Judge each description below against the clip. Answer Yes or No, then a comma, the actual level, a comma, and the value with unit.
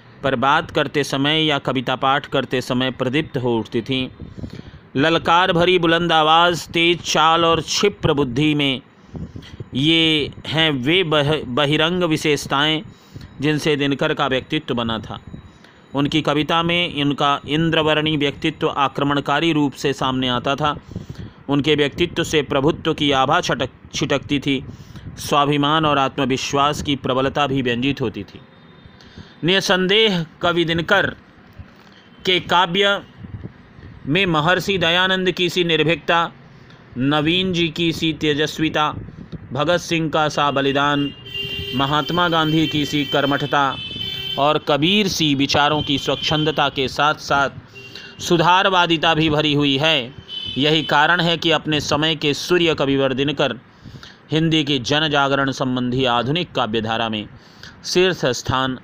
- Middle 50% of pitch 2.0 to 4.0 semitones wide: Yes, average, 3.1 semitones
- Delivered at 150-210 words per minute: No, average, 125 wpm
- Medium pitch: Yes, medium, 150 Hz